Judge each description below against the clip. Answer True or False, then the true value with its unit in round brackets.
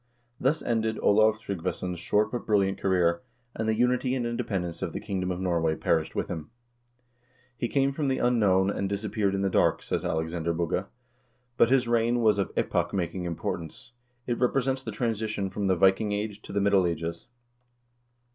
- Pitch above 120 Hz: False (100 Hz)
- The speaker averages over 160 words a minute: True (185 wpm)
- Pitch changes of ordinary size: True (4.5 semitones)